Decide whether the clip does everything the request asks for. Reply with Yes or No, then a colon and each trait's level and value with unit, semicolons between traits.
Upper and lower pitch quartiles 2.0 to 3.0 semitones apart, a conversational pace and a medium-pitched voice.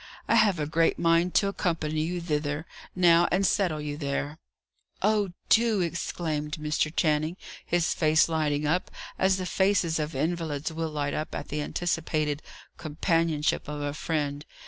Yes: average, 2.7 semitones; average, 155 wpm; medium, 160 Hz